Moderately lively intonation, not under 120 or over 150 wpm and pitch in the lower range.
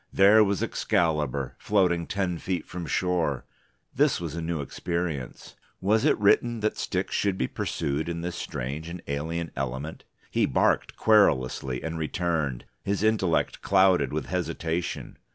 Yes: average, 3.7 semitones; average, 145 wpm; very low, 85 Hz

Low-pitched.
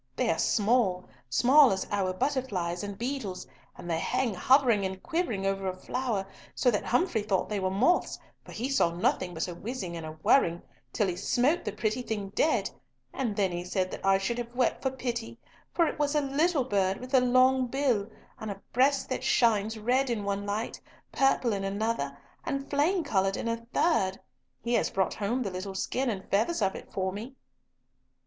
No: high, 220 Hz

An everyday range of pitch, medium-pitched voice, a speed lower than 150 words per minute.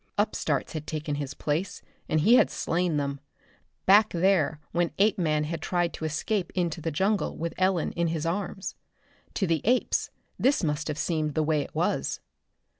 No: average, 3.6 semitones; medium, 165 Hz; average, 175 wpm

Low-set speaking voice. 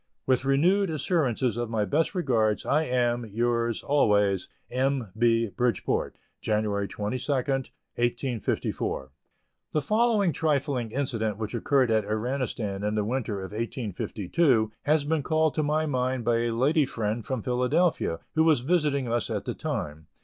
Yes: low, 125 Hz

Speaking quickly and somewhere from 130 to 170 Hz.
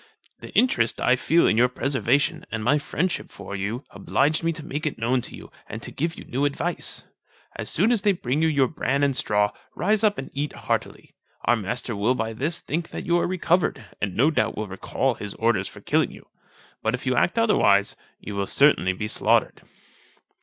Yes: fast, 210 wpm; low, 135 Hz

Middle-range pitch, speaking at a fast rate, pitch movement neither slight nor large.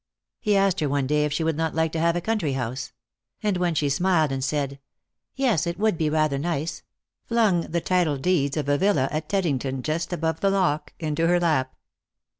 Yes: medium, 160 Hz; fast, 215 wpm; average, 3.8 semitones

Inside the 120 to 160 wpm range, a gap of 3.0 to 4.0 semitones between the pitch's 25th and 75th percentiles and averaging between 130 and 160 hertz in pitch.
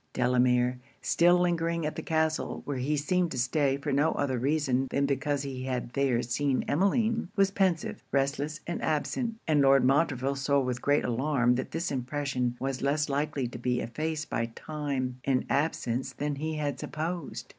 No: average, 175 wpm; average, 3.3 semitones; medium, 140 Hz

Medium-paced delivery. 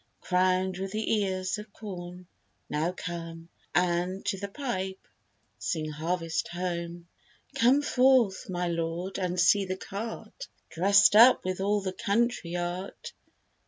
No: slow, 130 wpm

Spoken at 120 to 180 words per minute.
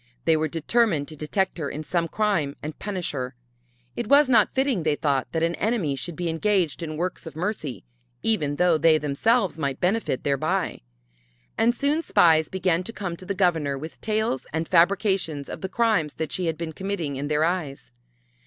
No: average, 190 wpm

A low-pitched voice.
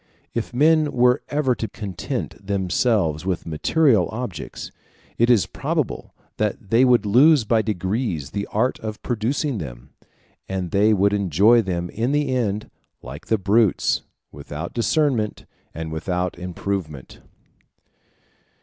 Yes: low, 105 Hz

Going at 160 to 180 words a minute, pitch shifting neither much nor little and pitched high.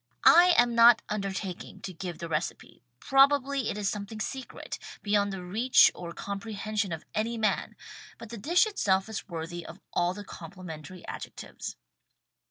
Yes: average, 165 wpm; average, 4.5 semitones; high, 205 Hz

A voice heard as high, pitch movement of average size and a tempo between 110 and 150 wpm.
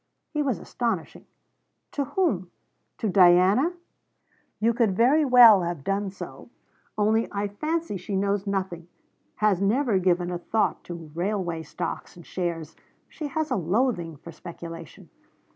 Yes: high, 195 Hz; average, 5.0 semitones; average, 140 wpm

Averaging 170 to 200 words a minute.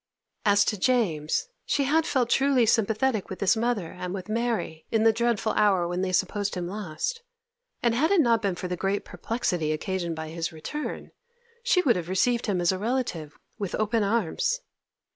Yes: average, 185 wpm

